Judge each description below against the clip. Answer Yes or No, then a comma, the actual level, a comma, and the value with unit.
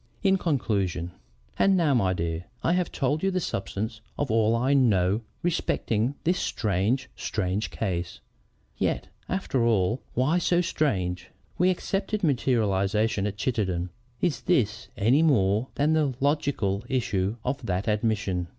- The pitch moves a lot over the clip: Yes, wide, 6.9 semitones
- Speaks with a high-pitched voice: No, low, 115 Hz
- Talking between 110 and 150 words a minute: Yes, average, 140 wpm